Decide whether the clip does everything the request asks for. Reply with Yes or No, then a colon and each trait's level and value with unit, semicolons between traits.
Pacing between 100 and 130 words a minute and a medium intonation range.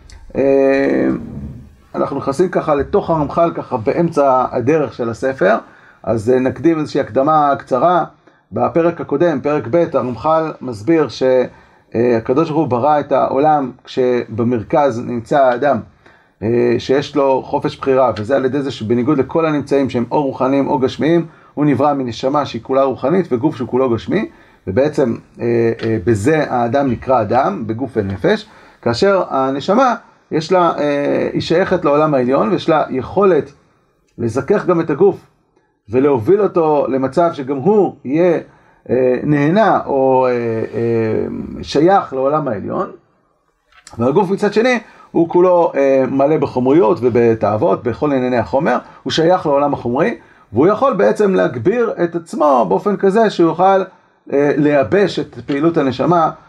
No: average, 140 wpm; average, 4.5 semitones